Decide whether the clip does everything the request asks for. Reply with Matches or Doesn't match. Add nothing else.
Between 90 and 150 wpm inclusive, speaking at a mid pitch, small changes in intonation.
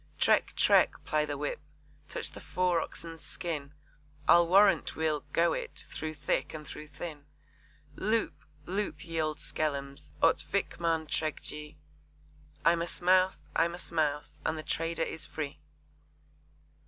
Matches